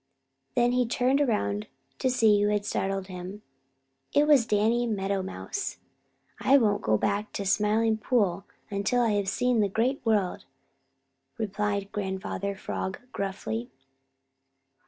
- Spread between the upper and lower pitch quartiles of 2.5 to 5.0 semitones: Yes, average, 3.2 semitones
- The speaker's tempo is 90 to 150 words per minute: Yes, average, 140 wpm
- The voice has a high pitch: Yes, high, 210 Hz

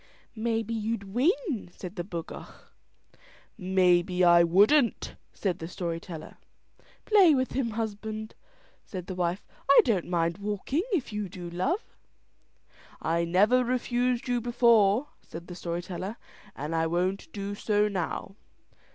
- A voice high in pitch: Yes, high, 200 Hz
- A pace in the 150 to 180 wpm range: No, slow, 135 wpm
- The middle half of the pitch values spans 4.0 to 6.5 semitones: Yes, average, 4.9 semitones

